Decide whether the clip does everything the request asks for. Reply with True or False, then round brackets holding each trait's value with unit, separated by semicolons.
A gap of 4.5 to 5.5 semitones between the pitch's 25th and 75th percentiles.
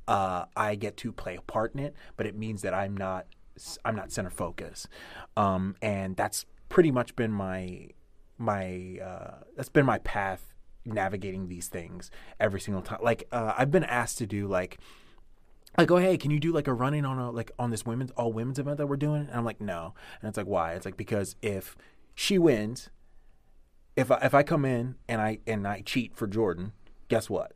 True (4.8 semitones)